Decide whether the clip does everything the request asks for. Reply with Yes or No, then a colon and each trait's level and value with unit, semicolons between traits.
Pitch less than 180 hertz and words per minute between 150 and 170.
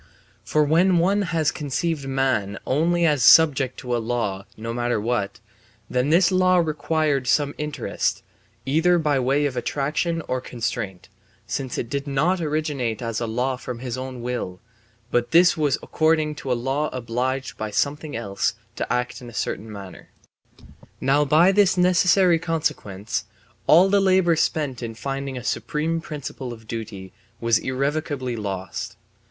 Yes: low, 135 Hz; average, 160 wpm